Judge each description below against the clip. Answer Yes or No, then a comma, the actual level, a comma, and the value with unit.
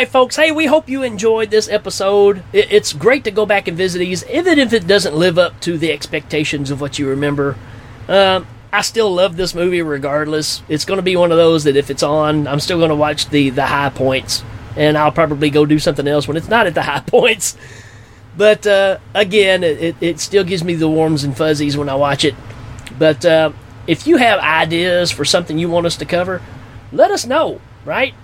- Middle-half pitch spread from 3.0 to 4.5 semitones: No, average, 5.3 semitones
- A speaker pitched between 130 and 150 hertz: No, medium, 165 Hz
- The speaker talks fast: Yes, fast, 220 wpm